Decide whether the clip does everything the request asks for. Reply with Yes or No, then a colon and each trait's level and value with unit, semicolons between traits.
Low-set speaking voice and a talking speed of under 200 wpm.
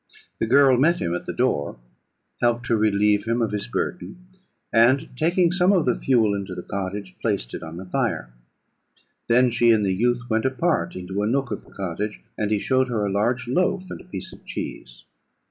No: low, 115 Hz; fast, 205 wpm